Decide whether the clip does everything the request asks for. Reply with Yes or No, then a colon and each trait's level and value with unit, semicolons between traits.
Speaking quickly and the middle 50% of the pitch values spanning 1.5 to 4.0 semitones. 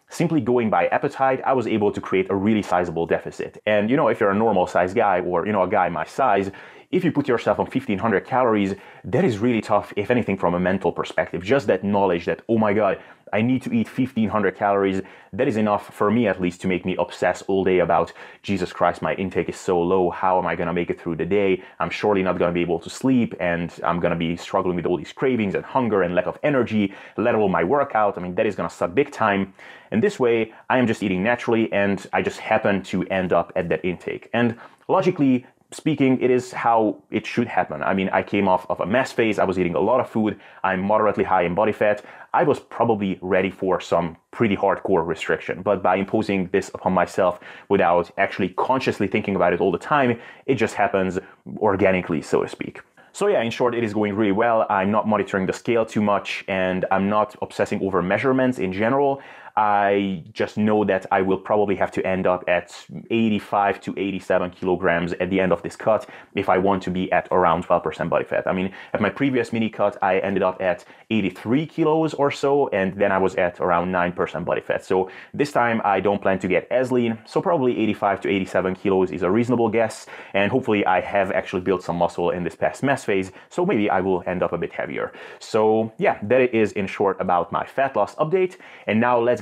Yes: fast, 230 wpm; average, 3.6 semitones